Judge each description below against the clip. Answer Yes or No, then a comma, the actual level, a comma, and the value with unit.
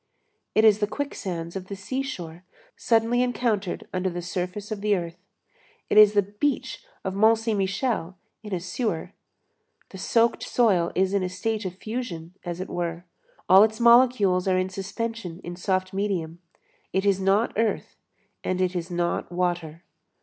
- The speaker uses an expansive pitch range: No, average, 3.4 semitones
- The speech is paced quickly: No, average, 170 wpm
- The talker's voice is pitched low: No, high, 190 Hz